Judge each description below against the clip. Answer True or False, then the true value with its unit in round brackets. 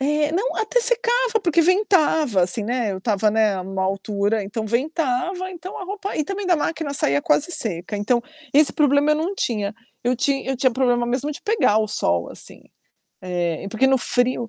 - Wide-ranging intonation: True (7.8 semitones)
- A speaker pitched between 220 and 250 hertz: False (260 Hz)